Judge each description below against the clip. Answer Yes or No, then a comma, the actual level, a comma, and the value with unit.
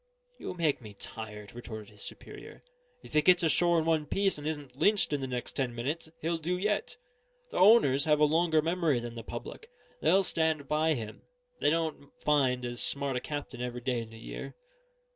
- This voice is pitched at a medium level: Yes, medium, 145 Hz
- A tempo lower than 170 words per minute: No, average, 200 wpm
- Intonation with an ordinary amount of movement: Yes, average, 5.0 semitones